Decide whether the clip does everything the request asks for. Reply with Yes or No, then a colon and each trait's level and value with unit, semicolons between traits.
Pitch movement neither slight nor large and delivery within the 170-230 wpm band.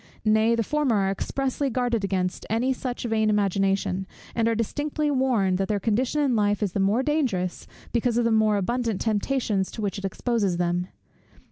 Yes: average, 4.0 semitones; average, 180 wpm